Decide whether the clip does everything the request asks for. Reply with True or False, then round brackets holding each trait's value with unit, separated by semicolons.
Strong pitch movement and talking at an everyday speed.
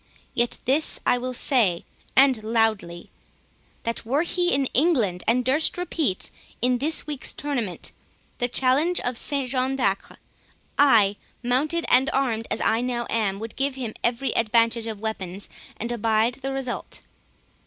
False (3.4 semitones; 150 wpm)